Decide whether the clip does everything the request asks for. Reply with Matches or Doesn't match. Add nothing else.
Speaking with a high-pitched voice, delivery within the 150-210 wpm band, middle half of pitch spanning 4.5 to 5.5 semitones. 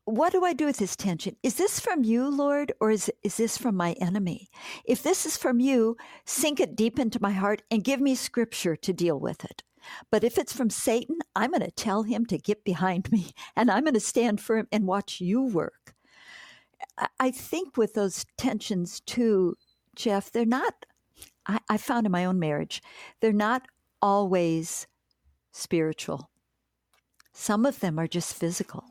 Matches